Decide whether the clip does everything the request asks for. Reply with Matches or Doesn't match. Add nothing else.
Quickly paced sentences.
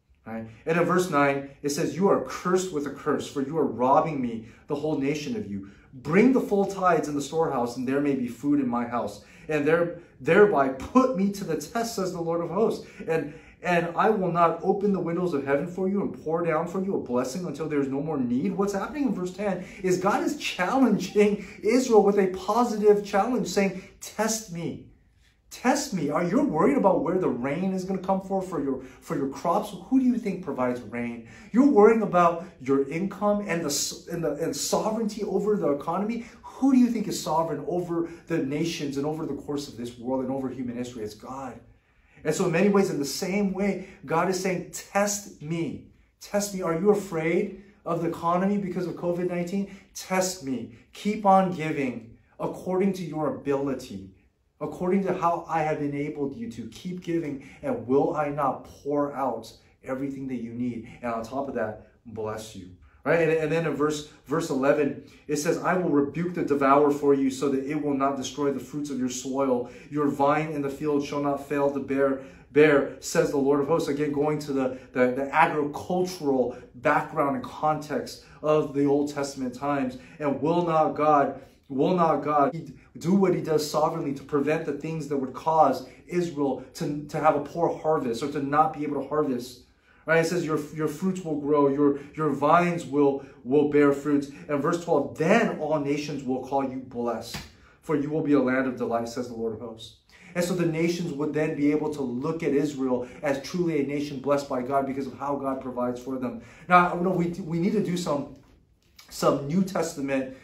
Matches